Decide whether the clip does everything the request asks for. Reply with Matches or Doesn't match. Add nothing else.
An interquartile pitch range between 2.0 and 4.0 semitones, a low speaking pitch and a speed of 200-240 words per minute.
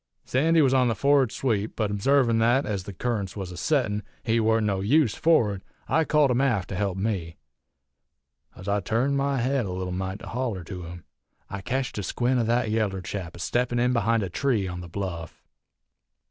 Doesn't match